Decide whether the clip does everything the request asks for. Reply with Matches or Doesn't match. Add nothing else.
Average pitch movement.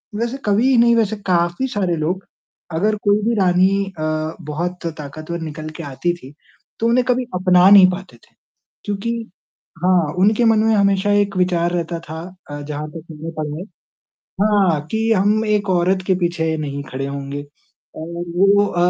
Matches